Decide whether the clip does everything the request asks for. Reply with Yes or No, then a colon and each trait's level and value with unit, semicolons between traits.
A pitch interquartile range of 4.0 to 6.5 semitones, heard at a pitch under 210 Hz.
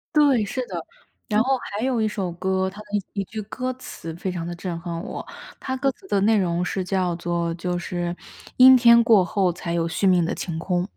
Yes: average, 4.6 semitones; high, 190 Hz